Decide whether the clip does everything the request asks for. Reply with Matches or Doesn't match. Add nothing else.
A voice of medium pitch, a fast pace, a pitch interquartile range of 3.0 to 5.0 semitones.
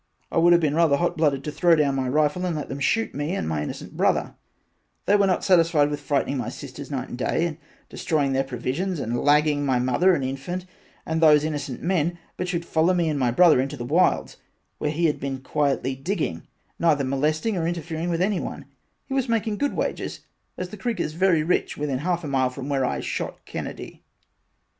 Matches